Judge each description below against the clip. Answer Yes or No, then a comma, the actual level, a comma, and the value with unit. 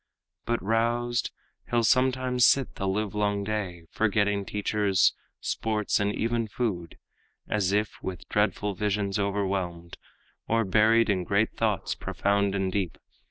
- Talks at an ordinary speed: No, slow, 125 wpm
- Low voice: Yes, low, 105 Hz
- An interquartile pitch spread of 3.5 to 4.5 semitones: No, narrow, 2.4 semitones